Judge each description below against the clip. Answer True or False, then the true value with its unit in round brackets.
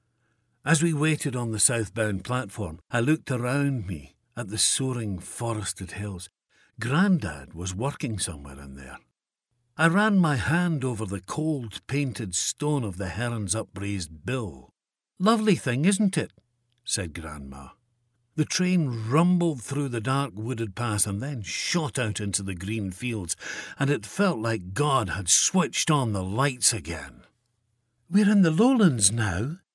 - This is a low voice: True (120 Hz)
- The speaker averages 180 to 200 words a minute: False (150 wpm)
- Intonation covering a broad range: True (6.3 semitones)